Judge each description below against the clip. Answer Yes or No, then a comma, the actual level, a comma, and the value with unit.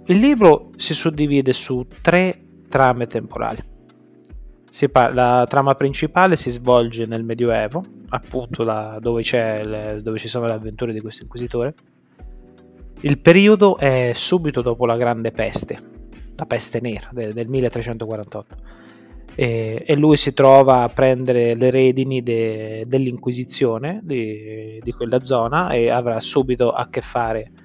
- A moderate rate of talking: Yes, average, 140 wpm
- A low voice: Yes, low, 120 Hz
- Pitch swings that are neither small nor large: Yes, average, 3.0 semitones